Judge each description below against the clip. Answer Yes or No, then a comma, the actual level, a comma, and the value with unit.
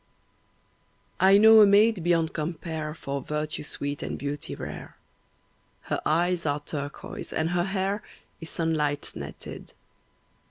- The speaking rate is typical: No, slow, 125 wpm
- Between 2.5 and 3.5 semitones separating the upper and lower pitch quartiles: No, average, 3.9 semitones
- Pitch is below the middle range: No, medium, 165 Hz